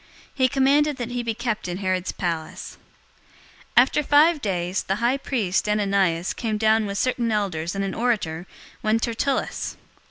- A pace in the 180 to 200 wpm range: No, average, 160 wpm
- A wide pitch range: No, average, 4.6 semitones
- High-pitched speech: Yes, high, 215 Hz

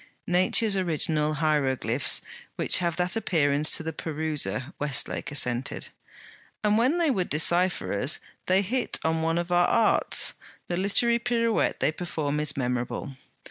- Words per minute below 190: Yes, average, 145 wpm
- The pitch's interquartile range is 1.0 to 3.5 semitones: No, average, 4.4 semitones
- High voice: No, medium, 160 Hz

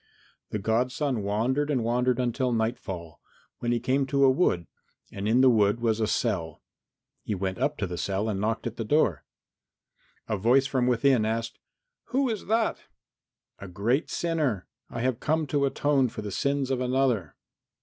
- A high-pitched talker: No, low, 120 Hz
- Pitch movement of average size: Yes, average, 4.2 semitones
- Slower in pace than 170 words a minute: No, average, 180 wpm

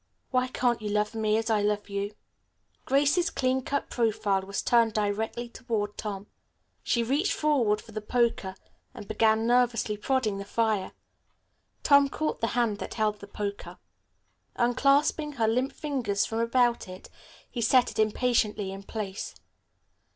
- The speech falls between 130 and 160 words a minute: Yes, average, 150 wpm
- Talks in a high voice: Yes, high, 225 Hz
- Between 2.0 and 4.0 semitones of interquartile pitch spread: Yes, average, 3.2 semitones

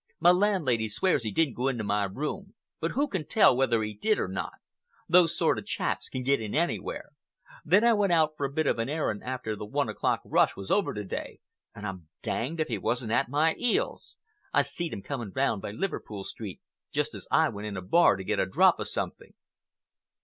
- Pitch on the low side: Yes, low, 130 Hz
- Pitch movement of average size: No, wide, 8.1 semitones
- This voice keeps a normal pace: No, fast, 220 wpm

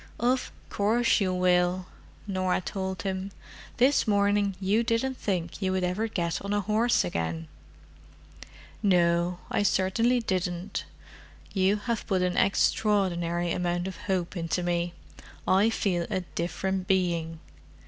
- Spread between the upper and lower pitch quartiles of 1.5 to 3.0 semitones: Yes, average, 2.7 semitones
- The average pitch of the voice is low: No, medium, 185 Hz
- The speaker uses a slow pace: Yes, slow, 130 wpm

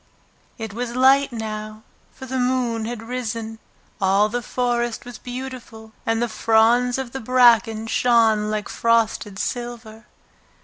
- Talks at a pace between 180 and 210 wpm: No, slow, 135 wpm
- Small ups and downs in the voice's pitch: Yes, narrow, 2.0 semitones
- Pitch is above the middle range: Yes, high, 230 Hz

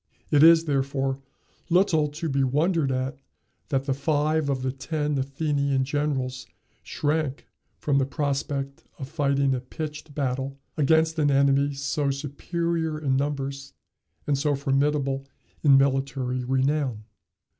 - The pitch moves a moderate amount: No, narrow, 1.9 semitones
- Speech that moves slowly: Yes, slow, 125 wpm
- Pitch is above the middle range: No, medium, 140 Hz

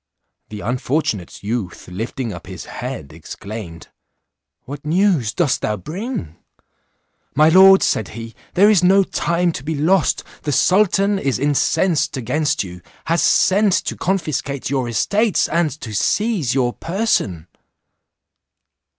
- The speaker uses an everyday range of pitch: No, wide, 8.5 semitones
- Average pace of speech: No, slow, 130 wpm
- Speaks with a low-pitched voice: No, medium, 145 Hz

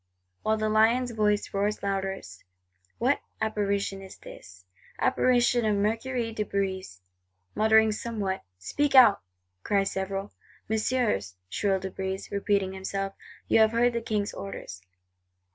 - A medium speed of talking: No, slow, 120 wpm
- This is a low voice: No, high, 205 Hz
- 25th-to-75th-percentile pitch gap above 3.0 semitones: No, narrow, 2.5 semitones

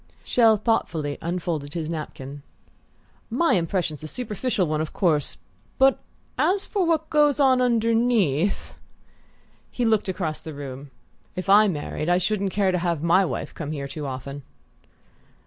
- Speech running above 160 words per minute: No, average, 150 wpm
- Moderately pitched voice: Yes, medium, 180 Hz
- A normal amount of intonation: No, wide, 6.9 semitones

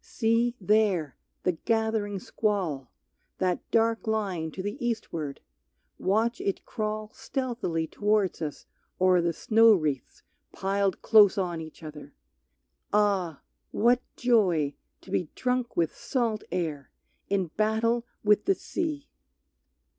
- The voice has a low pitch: No, high, 205 Hz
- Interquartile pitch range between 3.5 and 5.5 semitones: Yes, average, 4.8 semitones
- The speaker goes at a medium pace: No, slow, 120 wpm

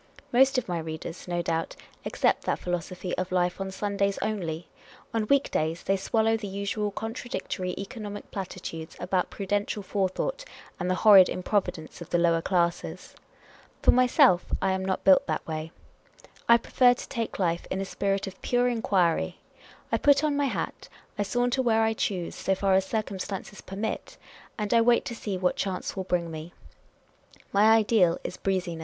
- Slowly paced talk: No, average, 175 wpm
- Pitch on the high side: Yes, high, 195 Hz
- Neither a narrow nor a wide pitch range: Yes, average, 3.6 semitones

